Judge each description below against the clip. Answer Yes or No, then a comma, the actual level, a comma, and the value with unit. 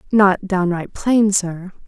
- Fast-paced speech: No, slow, 130 wpm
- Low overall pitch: No, high, 190 Hz